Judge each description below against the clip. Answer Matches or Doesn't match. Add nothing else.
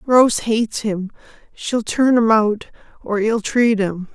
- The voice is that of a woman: Matches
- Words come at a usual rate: Doesn't match